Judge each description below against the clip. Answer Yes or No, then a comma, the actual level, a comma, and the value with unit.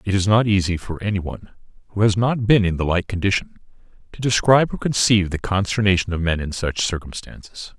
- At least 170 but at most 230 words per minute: Yes, average, 200 wpm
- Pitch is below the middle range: Yes, low, 100 Hz